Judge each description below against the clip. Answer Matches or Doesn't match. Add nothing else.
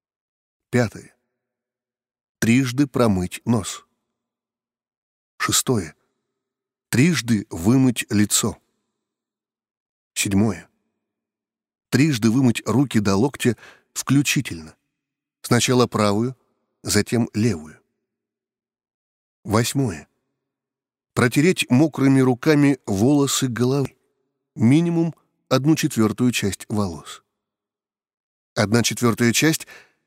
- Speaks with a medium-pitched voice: Doesn't match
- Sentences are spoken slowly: Matches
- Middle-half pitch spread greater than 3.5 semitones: Matches